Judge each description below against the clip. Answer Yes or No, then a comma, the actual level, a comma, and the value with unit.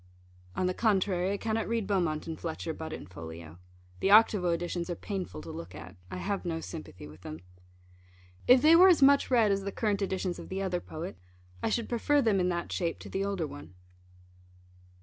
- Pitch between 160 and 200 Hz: Yes, medium, 185 Hz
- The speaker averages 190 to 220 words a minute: Yes, fast, 205 wpm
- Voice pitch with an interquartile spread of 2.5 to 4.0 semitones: No, average, 4.7 semitones